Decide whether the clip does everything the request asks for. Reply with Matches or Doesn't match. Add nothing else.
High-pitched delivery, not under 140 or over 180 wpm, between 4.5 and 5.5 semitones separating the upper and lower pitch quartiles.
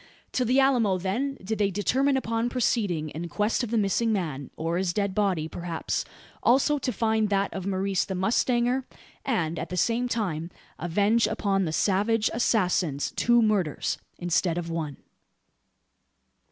Matches